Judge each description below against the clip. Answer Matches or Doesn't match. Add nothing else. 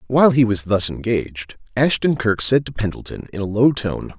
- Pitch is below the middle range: Matches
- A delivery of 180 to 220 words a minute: Matches